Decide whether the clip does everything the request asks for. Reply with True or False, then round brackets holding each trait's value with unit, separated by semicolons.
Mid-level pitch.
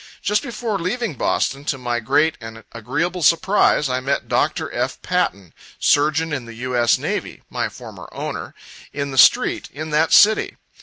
True (145 Hz)